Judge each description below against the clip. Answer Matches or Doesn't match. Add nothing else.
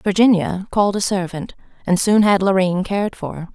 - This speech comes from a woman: Matches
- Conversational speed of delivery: Matches